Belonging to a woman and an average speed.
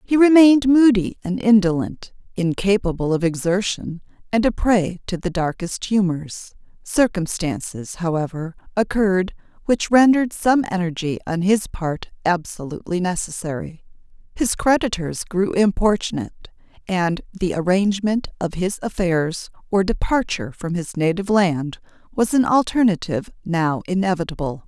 No: female; slow, 115 wpm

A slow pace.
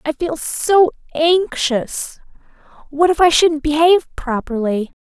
Yes: slow, 120 wpm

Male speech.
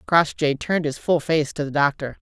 No: female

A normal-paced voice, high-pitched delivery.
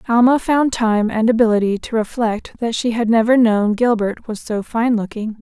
Yes: average, 185 wpm; high, 225 Hz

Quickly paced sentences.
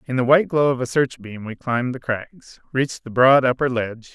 Yes: fast, 230 wpm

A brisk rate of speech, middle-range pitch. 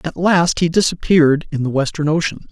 No: average, 190 wpm; medium, 160 Hz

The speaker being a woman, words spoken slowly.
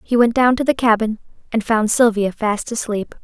No: female; fast, 205 wpm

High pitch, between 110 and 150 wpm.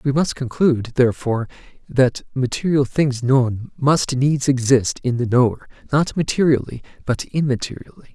No: low, 130 Hz; slow, 135 wpm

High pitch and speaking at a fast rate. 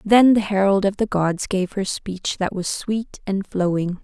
Yes: high, 195 Hz; fast, 210 wpm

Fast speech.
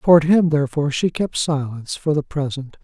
No: average, 190 wpm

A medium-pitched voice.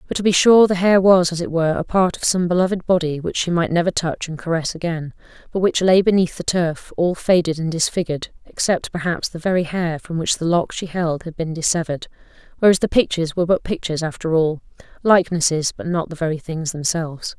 Yes: medium, 170 Hz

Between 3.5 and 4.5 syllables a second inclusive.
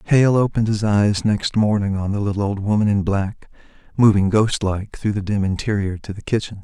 No: 5.3 syllables/s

